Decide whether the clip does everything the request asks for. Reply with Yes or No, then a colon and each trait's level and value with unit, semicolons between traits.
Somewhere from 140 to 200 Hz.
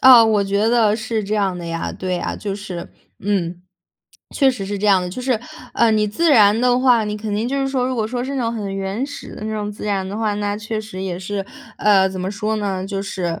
No: high, 210 Hz